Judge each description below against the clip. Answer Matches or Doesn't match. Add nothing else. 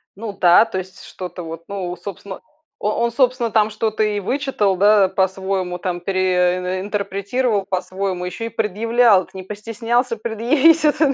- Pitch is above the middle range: Matches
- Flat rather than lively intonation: Doesn't match